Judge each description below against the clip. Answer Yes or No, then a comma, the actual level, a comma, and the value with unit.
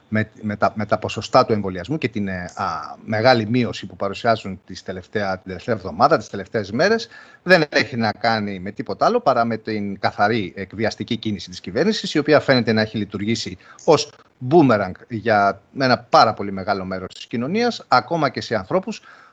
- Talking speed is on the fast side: Yes, fast, 180 wpm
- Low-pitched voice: Yes, low, 110 Hz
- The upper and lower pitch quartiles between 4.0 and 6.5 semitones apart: Yes, average, 4.3 semitones